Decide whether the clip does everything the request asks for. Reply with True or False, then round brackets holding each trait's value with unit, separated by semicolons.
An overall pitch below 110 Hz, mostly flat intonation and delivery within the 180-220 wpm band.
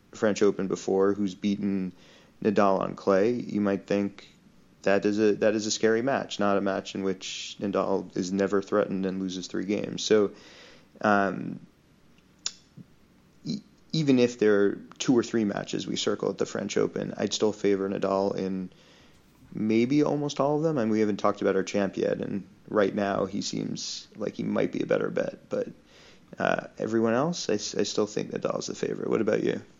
True (100 Hz; 2.1 semitones; 190 wpm)